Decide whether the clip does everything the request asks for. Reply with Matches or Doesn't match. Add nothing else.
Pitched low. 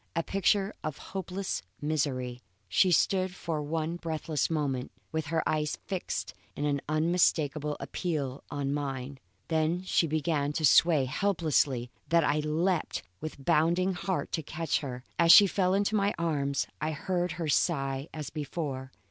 Doesn't match